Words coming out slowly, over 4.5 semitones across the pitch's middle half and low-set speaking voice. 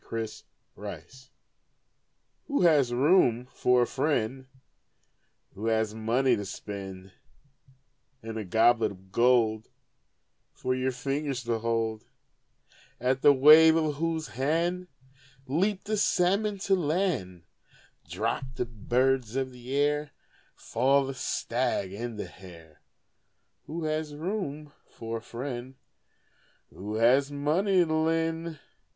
Yes: slow, 120 wpm; wide, 5.6 semitones; low, 130 Hz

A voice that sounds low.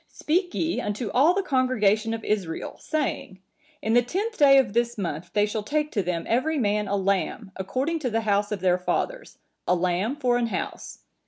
No: high, 225 Hz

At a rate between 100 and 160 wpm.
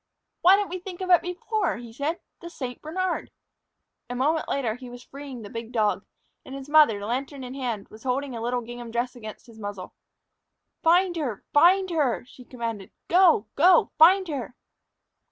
No: average, 180 wpm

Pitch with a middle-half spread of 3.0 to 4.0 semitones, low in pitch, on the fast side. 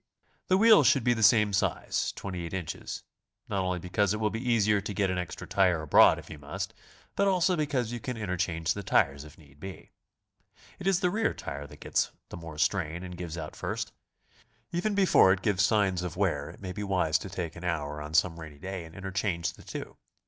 No: average, 4.8 semitones; very low, 95 Hz; fast, 215 wpm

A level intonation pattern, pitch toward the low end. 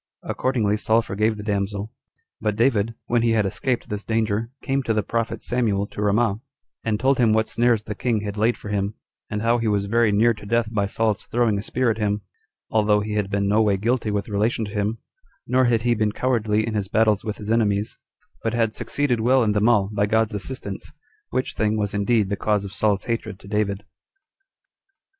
Yes: narrow, 2.1 semitones; low, 110 Hz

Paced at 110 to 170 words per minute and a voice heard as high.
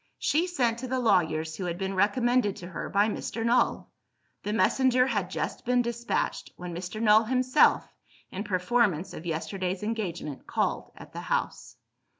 Yes: average, 160 wpm; high, 210 Hz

